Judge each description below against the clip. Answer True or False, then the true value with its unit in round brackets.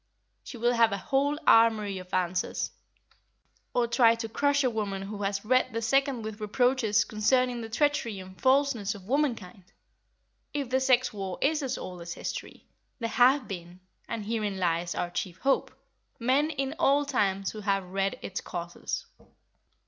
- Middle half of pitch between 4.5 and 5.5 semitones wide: True (5.0 semitones)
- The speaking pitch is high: True (225 Hz)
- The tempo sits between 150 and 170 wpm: True (160 wpm)